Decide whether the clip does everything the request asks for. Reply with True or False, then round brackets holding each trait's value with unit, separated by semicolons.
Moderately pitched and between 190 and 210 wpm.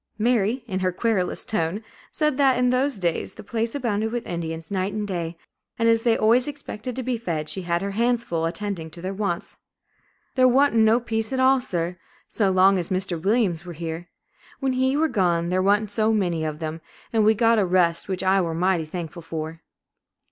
False (200 Hz; 205 wpm)